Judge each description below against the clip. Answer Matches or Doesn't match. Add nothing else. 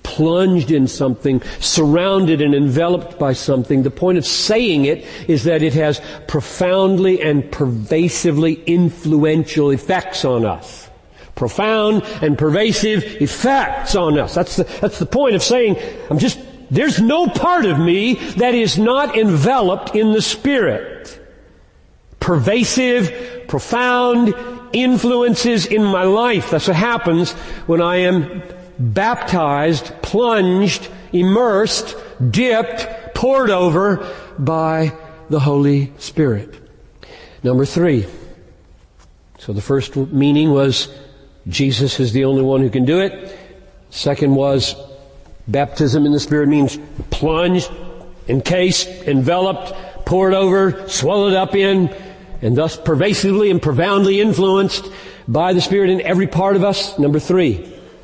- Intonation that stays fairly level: Doesn't match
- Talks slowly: Matches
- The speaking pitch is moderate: Matches